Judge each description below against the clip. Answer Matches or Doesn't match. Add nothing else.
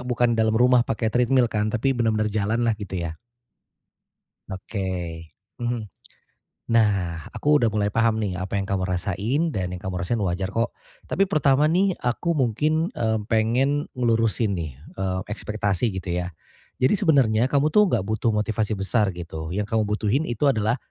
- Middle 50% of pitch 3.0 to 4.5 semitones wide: Matches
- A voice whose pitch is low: Matches